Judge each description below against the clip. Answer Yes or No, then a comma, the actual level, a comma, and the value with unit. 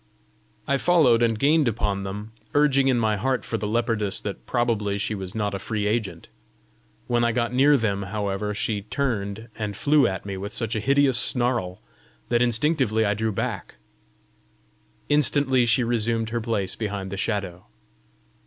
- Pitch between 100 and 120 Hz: Yes, low, 110 Hz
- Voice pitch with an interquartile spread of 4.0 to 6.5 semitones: No, average, 3.3 semitones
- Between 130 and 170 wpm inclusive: Yes, average, 165 wpm